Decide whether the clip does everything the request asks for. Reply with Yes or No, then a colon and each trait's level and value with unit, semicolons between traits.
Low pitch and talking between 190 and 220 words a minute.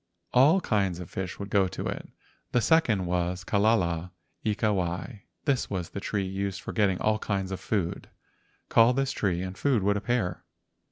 No: low, 100 Hz; average, 175 wpm